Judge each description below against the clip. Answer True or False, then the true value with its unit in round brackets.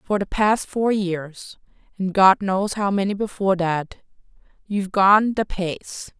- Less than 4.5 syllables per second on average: True (4.0 syllables/s)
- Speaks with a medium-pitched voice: False (195 Hz)